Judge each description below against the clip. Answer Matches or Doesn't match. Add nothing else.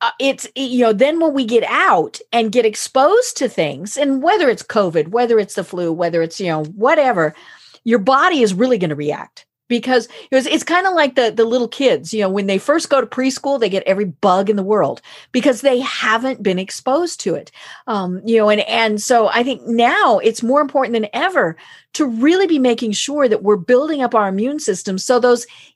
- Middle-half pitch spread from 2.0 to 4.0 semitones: Doesn't match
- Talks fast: Matches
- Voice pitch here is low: Doesn't match